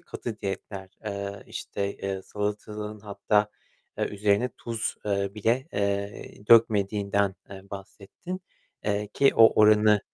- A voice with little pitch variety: Yes, narrow, 1.2 semitones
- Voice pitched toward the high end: No, low, 105 Hz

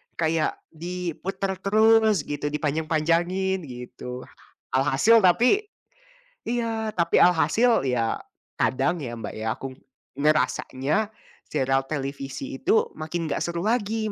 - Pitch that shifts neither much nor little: No, wide, 7.5 semitones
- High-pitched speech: No, medium, 165 Hz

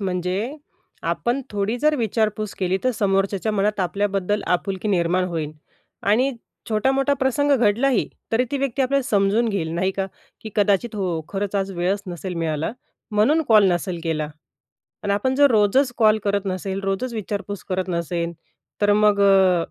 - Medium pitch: No, high, 200 Hz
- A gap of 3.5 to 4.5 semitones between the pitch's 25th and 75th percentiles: No, average, 3.1 semitones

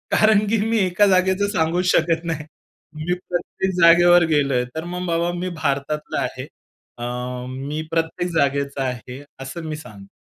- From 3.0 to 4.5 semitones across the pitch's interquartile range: Yes, average, 4.1 semitones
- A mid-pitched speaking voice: Yes, medium, 165 Hz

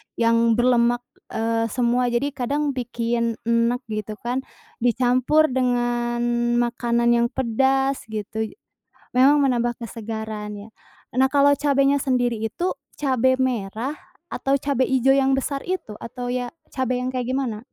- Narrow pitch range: Yes, narrow, 2.3 semitones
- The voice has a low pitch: No, high, 245 Hz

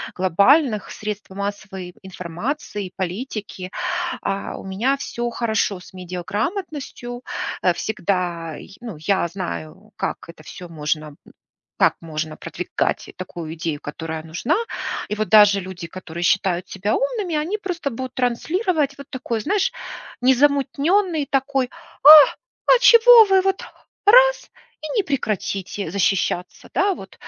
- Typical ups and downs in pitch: No, wide, 8.0 semitones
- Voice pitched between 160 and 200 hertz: No, high, 210 Hz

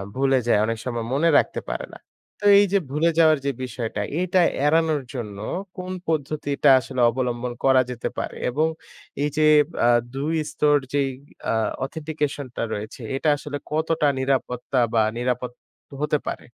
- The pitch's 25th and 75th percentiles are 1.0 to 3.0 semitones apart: No, average, 3.7 semitones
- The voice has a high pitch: No, medium, 140 Hz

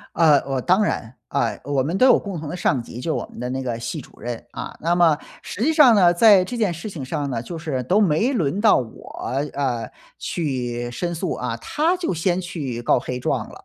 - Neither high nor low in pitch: Yes, medium, 155 Hz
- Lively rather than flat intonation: Yes, wide, 6.6 semitones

